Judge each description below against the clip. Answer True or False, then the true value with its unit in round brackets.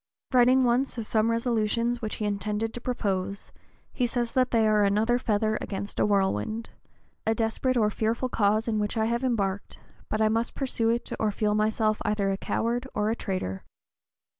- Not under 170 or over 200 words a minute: True (185 wpm)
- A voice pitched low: False (220 Hz)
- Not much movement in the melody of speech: True (2.2 semitones)